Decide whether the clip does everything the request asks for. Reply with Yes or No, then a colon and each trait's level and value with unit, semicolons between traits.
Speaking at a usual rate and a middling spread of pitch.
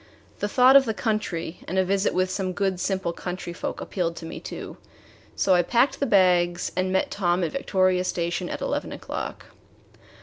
No: average, 190 wpm; narrow, 2.1 semitones